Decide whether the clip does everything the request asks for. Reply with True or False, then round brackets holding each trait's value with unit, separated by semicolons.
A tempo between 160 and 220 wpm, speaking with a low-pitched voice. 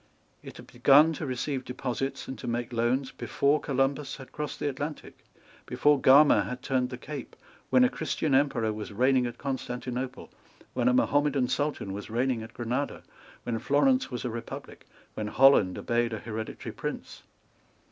True (165 wpm; 130 Hz)